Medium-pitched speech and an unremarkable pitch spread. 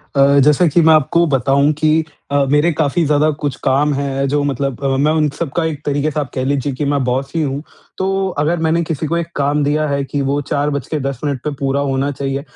No: medium, 145 Hz; narrow, 1.9 semitones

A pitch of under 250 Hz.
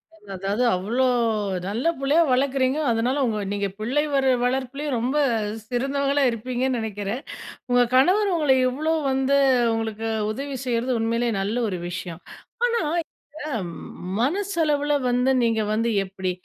No: very high, 255 Hz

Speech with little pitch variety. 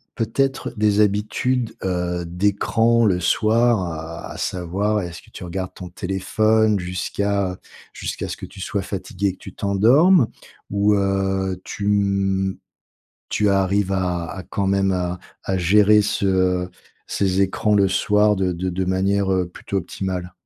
Yes: narrow, 2.2 semitones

